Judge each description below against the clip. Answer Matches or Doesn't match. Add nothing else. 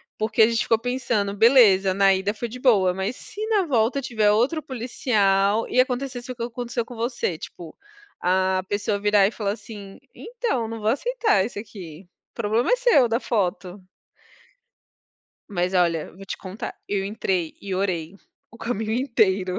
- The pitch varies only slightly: Doesn't match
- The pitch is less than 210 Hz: Doesn't match